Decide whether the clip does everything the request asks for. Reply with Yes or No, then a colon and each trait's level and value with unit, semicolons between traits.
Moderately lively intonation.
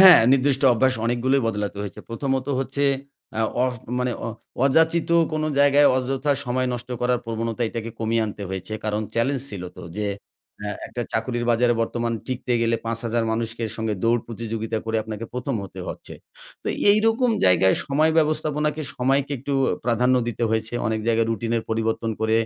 Yes: average, 3.2 semitones